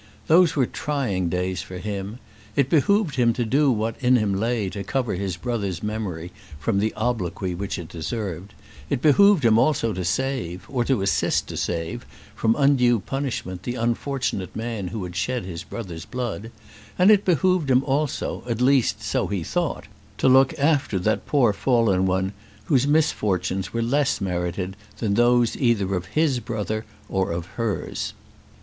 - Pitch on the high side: No, low, 115 Hz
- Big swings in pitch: Yes, wide, 5.8 semitones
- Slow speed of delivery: No, average, 170 wpm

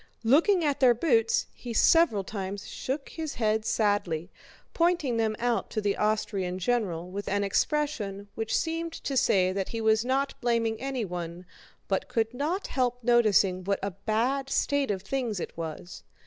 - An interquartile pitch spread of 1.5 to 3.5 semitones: No, average, 5.1 semitones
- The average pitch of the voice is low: No, high, 225 Hz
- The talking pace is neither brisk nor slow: Yes, average, 160 wpm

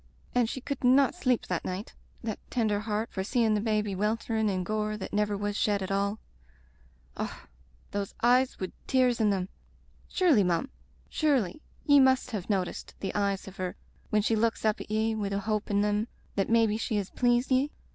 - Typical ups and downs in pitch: Yes, average, 3.2 semitones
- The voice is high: Yes, high, 215 Hz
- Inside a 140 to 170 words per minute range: No, fast, 205 wpm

